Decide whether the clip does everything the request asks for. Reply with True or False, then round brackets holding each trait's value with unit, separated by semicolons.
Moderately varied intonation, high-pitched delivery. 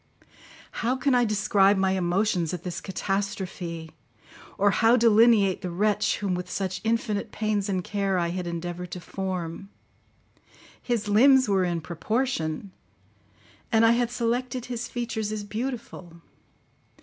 True (4.0 semitones; 200 Hz)